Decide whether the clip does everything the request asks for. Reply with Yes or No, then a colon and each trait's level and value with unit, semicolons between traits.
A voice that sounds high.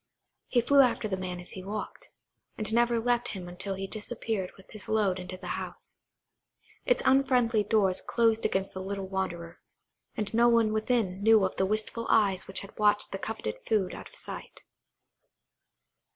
Yes: high, 210 Hz